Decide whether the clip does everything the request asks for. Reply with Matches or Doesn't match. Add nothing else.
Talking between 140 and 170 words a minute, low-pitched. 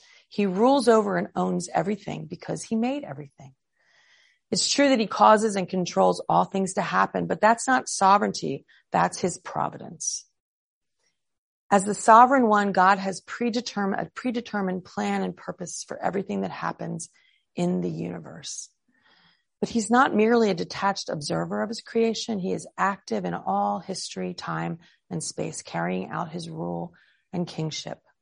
Doesn't match